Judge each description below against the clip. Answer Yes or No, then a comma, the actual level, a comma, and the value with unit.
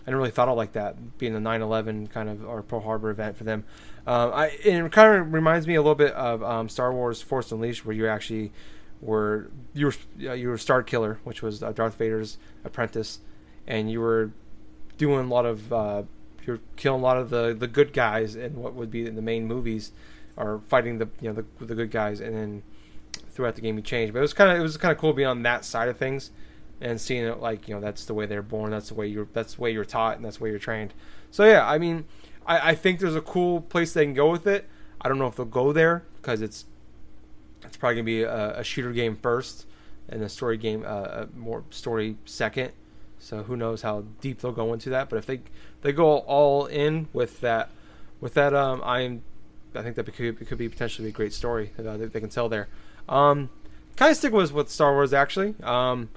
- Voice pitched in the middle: No, low, 115 Hz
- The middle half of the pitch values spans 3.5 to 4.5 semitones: Yes, average, 4.0 semitones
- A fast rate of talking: Yes, fast, 240 wpm